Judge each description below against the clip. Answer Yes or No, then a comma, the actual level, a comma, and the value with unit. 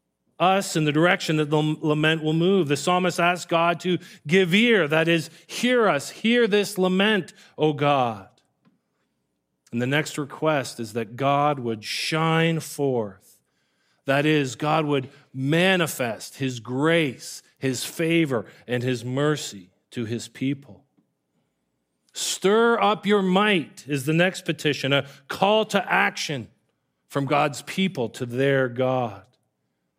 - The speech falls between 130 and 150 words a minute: Yes, slow, 135 wpm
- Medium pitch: Yes, medium, 150 Hz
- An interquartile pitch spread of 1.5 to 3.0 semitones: No, average, 5.0 semitones